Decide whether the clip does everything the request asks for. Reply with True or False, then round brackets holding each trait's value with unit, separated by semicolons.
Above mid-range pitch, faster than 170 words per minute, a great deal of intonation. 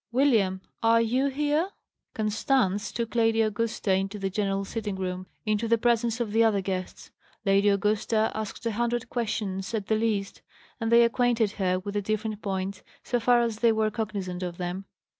False (215 Hz; 180 wpm; 2.8 semitones)